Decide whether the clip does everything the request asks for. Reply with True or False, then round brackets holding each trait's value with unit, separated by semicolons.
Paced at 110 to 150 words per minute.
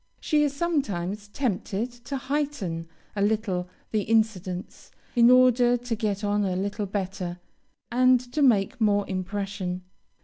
True (135 wpm)